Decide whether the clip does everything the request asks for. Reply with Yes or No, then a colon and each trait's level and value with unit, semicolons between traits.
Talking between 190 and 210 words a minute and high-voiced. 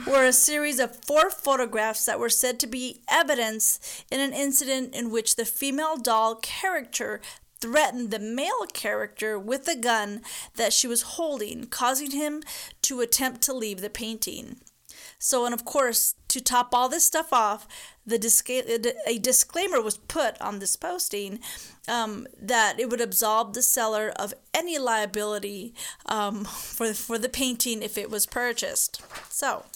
No: average, 160 wpm; high, 245 Hz